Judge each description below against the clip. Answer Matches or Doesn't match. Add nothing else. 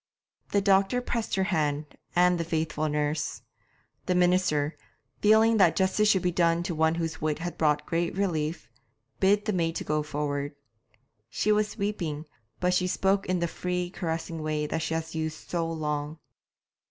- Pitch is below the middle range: Doesn't match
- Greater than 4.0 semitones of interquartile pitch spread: Doesn't match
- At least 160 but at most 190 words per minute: Matches